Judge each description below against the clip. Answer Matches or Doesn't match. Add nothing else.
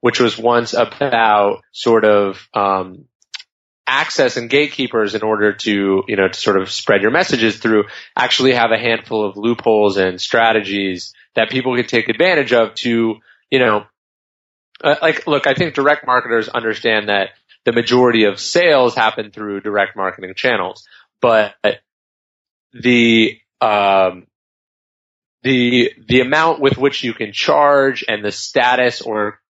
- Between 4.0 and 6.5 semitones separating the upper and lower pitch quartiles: Doesn't match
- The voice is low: Matches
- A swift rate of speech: Doesn't match